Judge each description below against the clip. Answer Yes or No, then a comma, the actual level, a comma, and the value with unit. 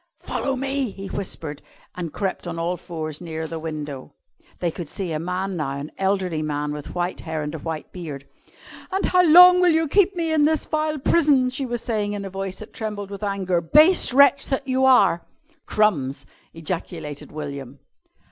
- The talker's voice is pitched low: No, high, 190 Hz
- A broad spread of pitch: Yes, wide, 8.8 semitones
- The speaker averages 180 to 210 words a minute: Yes, average, 185 wpm